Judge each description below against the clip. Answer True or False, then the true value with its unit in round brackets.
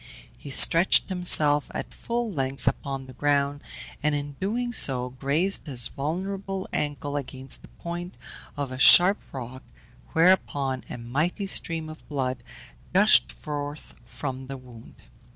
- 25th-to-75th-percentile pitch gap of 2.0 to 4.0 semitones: False (4.7 semitones)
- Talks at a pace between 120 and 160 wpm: True (135 wpm)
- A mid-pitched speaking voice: True (145 Hz)